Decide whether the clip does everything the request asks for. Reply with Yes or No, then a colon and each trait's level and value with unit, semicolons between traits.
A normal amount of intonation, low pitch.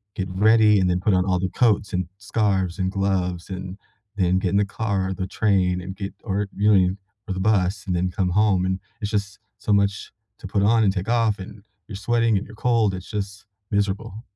No: narrow, 2.2 semitones; low, 100 Hz